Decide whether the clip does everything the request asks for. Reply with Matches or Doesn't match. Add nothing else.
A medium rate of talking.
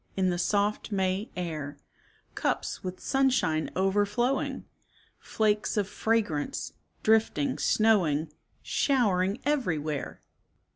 Doesn't match